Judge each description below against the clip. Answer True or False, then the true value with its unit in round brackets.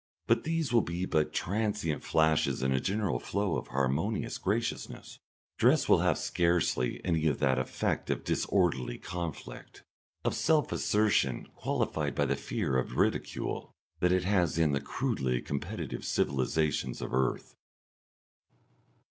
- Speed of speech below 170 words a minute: True (140 wpm)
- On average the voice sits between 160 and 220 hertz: False (80 Hz)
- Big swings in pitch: True (7.1 semitones)